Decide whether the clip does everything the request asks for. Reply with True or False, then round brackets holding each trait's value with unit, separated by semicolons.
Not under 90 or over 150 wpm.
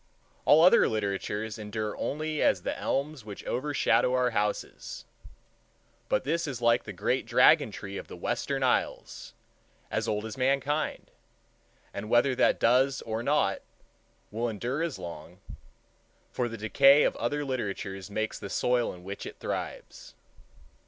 True (145 wpm)